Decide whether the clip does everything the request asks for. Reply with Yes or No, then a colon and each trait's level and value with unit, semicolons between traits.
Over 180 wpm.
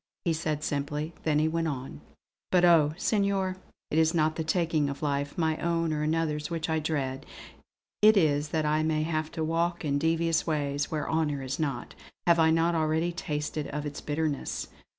Yes: average, 190 wpm